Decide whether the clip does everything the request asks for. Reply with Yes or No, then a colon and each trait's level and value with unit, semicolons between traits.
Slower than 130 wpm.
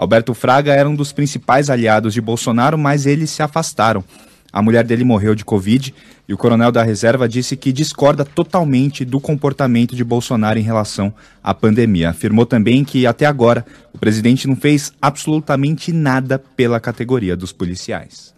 No: average, 165 wpm